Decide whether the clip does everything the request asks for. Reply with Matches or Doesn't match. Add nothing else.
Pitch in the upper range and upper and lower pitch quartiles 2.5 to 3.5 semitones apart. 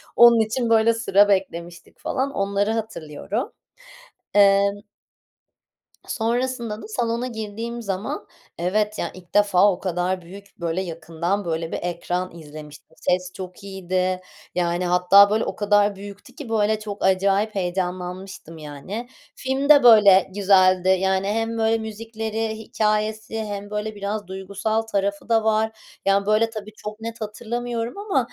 Matches